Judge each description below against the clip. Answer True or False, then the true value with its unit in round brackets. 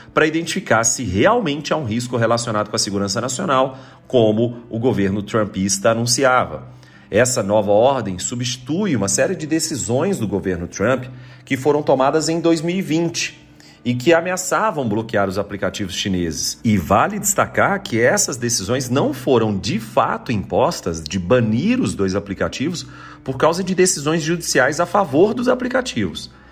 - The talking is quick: False (145 wpm)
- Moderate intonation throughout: False (7.1 semitones)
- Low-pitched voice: True (125 Hz)